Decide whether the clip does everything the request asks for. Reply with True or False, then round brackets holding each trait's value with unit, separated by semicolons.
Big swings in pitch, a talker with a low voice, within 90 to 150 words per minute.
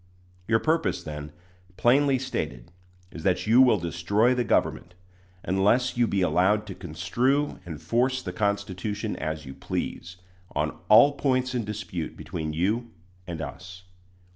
True (5.8 semitones; 100 Hz; 140 wpm)